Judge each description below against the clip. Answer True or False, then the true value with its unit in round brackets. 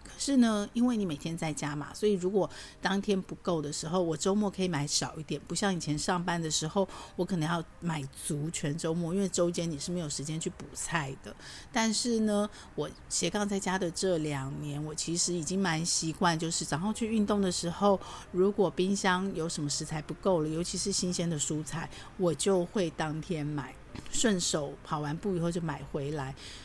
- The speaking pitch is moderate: True (170 Hz)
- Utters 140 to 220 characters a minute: False (290 characters per minute)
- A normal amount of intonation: True (3.7 semitones)